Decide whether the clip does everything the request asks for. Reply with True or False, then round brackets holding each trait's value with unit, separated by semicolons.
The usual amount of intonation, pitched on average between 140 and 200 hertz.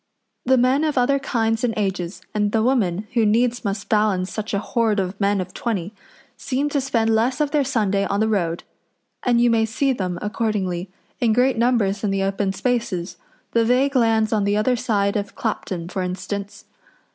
False (3.6 semitones; 220 Hz)